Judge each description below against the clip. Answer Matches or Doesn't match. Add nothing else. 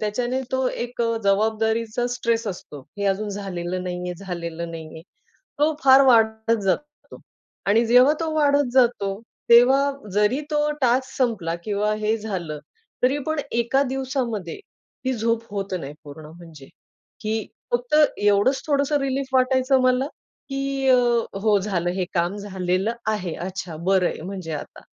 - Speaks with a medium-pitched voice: Doesn't match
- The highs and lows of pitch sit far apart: Matches